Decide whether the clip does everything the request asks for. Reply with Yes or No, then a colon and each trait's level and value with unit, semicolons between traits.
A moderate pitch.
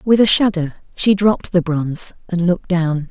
Yes: medium, 180 Hz